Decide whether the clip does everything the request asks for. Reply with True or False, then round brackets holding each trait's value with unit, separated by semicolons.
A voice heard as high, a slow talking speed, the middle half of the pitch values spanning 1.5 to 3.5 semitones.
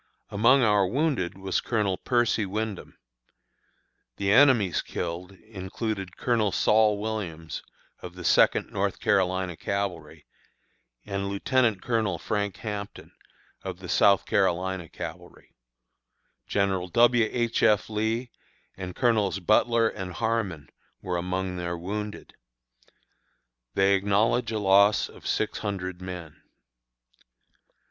False (100 Hz; 110 wpm; 3.1 semitones)